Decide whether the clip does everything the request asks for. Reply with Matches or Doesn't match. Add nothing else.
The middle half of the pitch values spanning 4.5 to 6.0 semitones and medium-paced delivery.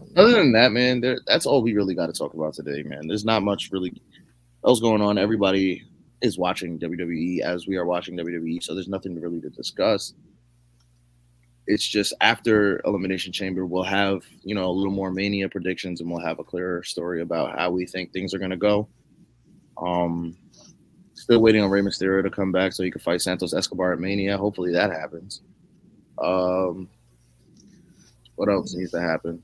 Doesn't match